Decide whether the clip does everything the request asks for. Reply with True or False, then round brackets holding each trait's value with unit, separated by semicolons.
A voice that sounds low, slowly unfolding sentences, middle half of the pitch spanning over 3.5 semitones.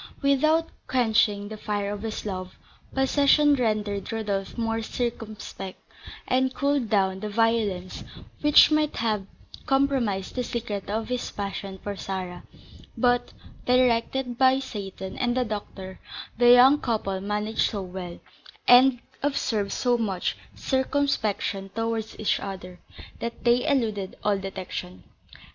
False (220 Hz; 125 wpm; 4.0 semitones)